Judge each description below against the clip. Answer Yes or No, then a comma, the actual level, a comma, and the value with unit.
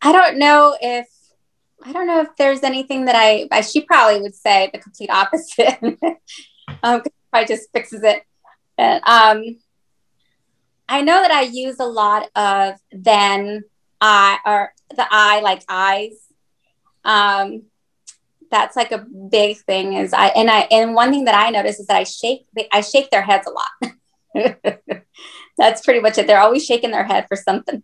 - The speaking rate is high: No, average, 170 wpm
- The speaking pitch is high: Yes, high, 225 Hz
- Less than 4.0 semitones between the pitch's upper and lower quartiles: No, average, 4.3 semitones